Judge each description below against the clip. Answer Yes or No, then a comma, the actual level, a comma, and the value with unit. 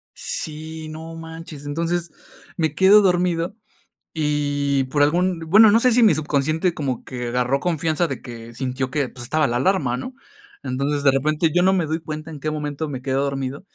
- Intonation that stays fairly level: No, average, 3.3 semitones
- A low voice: No, medium, 155 Hz